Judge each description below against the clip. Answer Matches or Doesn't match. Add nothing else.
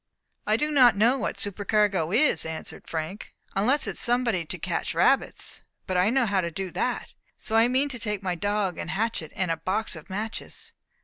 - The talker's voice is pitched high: Matches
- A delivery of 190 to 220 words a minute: Matches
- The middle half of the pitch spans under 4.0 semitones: Doesn't match